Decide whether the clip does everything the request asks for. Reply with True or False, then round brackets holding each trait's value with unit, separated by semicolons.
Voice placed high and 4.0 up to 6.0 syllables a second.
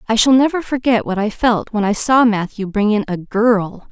True (220 Hz; 5.2 syllables/s)